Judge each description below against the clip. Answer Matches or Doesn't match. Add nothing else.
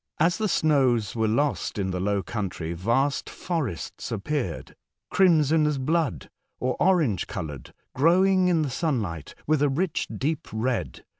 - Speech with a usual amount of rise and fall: Doesn't match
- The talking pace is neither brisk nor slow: Matches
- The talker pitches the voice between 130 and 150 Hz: Matches